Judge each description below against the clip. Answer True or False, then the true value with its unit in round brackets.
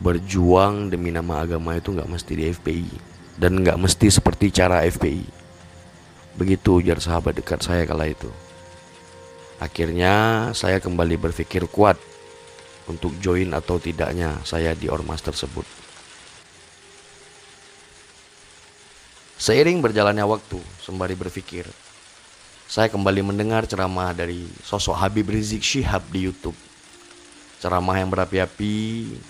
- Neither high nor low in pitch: False (90 Hz)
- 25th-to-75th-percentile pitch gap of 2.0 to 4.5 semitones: True (2.7 semitones)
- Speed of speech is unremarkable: True (110 wpm)